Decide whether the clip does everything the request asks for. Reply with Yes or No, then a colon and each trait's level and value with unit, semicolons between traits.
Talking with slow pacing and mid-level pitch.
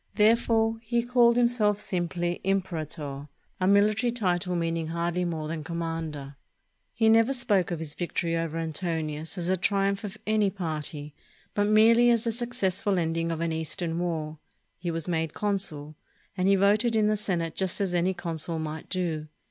No: average, 170 wpm; medium, 180 Hz